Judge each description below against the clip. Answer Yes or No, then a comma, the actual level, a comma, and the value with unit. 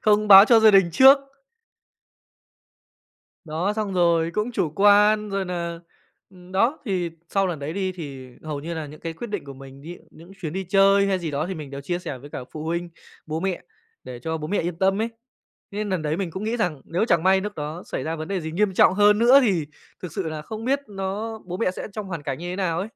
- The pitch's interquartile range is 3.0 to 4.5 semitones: Yes, average, 4.1 semitones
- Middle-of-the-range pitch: Yes, medium, 180 Hz